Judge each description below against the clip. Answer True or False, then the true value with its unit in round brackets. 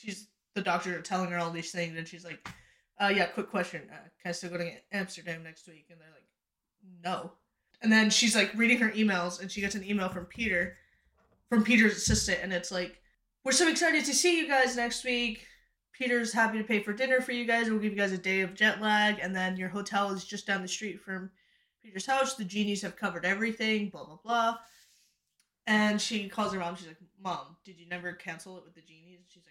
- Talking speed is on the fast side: True (230 wpm)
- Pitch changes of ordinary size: True (3.8 semitones)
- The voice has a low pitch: False (200 Hz)